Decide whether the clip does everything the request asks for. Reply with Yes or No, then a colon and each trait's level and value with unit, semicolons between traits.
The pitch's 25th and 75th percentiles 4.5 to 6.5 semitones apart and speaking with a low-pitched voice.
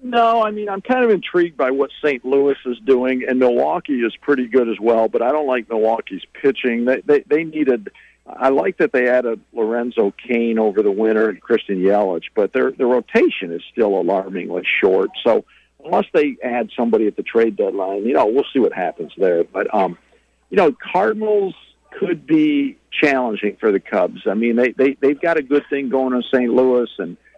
Yes: average, 5.0 semitones; low, 130 Hz